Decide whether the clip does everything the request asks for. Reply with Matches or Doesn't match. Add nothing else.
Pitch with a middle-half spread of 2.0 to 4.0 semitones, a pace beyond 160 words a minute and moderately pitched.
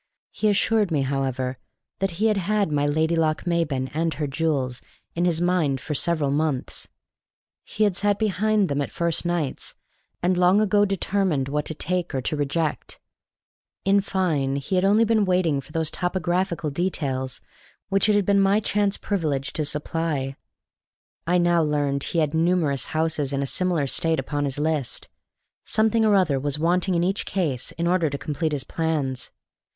Doesn't match